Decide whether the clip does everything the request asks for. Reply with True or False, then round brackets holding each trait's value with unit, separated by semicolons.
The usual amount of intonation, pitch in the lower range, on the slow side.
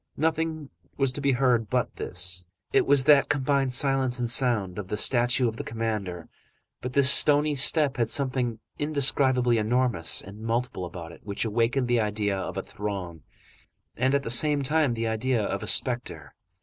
False (4.3 semitones; 125 Hz; 175 wpm)